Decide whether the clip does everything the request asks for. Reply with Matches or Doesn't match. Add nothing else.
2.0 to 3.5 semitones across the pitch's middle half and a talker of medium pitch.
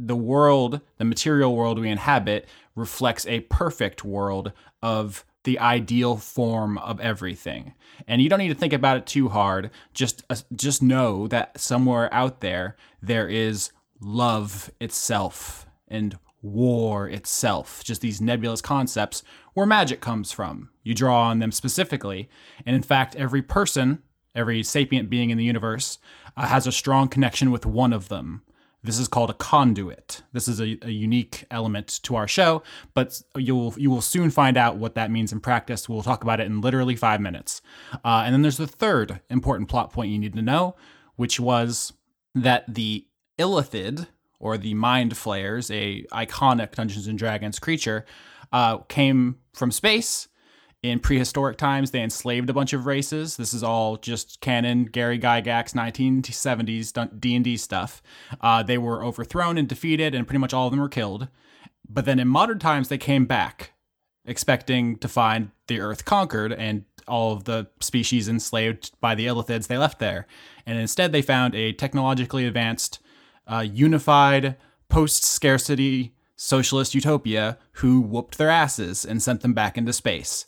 Doesn't match